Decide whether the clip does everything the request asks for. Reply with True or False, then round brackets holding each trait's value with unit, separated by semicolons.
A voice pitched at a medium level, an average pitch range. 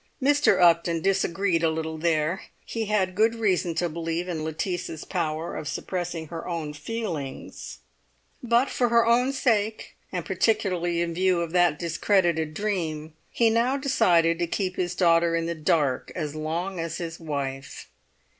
True (170 Hz; 3.7 semitones)